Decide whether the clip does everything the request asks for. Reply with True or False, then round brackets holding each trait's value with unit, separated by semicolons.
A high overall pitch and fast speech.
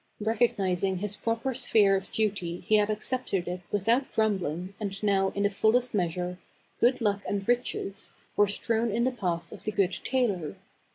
False (205 Hz; 180 wpm)